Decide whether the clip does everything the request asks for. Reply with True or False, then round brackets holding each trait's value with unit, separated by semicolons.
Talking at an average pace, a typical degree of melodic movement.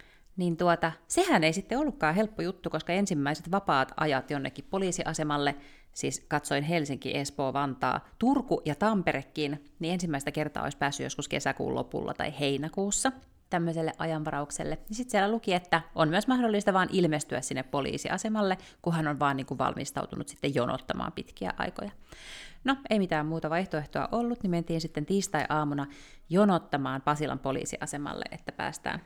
True (145 wpm; 4.9 semitones)